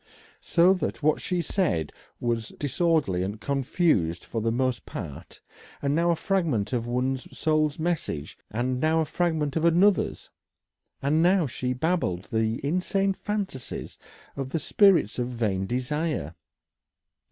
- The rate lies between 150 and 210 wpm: No, slow, 135 wpm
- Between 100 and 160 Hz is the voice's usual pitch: Yes, medium, 140 Hz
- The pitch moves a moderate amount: No, wide, 6.3 semitones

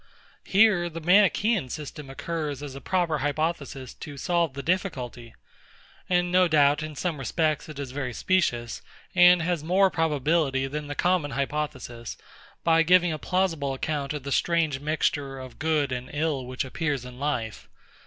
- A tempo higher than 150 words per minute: Yes, average, 160 wpm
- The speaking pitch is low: No, medium, 150 Hz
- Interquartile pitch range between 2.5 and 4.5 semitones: Yes, average, 4.0 semitones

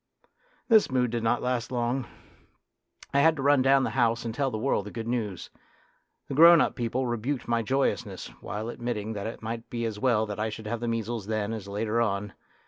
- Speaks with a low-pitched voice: Yes, low, 115 Hz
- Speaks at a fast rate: Yes, fast, 215 wpm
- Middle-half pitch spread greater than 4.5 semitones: No, average, 2.8 semitones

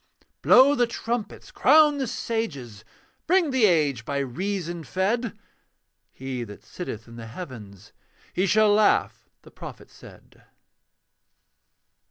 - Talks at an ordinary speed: No, slow, 120 wpm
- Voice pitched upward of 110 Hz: Yes, medium, 185 Hz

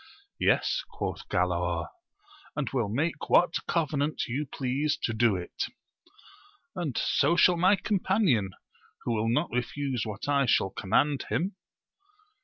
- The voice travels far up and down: Yes, wide, 6.2 semitones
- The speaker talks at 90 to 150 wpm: Yes, slow, 135 wpm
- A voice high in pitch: No, medium, 140 Hz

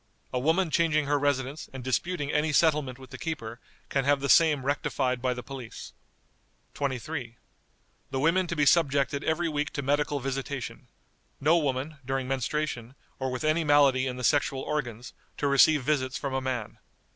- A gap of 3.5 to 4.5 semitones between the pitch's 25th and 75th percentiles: No, narrow, 2.6 semitones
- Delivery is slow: No, average, 170 wpm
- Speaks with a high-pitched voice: No, medium, 140 Hz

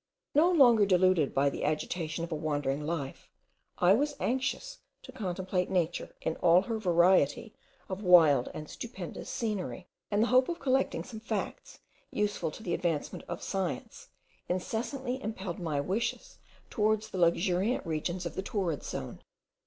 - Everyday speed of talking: Yes, average, 155 wpm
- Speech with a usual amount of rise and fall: Yes, average, 4.9 semitones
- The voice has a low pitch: No, medium, 185 Hz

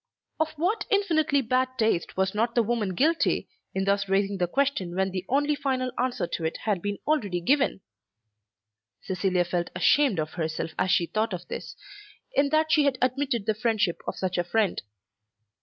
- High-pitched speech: Yes, high, 220 Hz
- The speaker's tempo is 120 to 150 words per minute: No, average, 180 wpm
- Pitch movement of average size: No, wide, 7.0 semitones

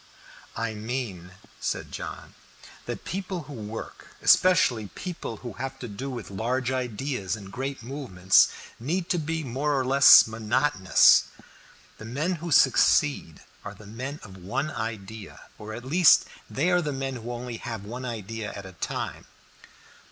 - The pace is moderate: Yes, average, 155 wpm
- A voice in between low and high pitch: No, low, 120 Hz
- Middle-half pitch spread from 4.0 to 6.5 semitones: Yes, average, 4.4 semitones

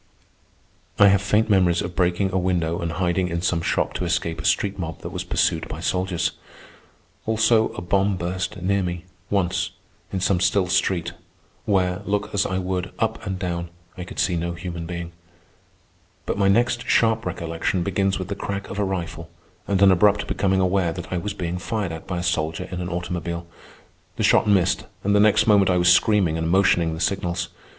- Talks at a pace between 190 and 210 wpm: Yes, average, 195 wpm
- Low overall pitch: Yes, very low, 90 Hz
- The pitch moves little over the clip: Yes, narrow, 2.3 semitones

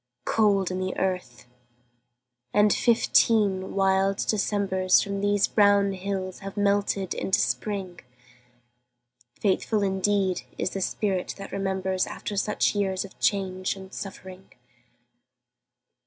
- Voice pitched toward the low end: No, high, 195 Hz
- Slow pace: Yes, slow, 110 wpm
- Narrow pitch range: Yes, narrow, 1.3 semitones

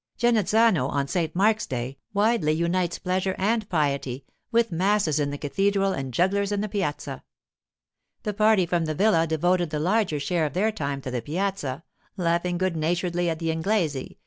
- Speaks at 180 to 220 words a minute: No, average, 170 wpm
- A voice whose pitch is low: No, medium, 175 Hz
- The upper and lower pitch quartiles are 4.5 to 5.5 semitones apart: Yes, average, 4.8 semitones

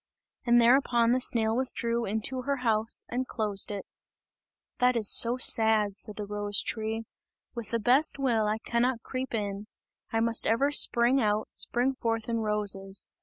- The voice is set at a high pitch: Yes, high, 230 Hz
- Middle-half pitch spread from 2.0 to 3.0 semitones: Yes, narrow, 2.5 semitones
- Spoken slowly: No, average, 165 wpm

